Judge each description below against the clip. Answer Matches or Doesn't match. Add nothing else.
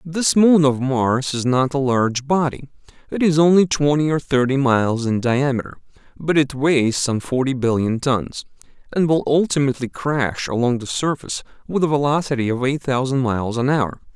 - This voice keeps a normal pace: Matches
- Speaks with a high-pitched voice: Doesn't match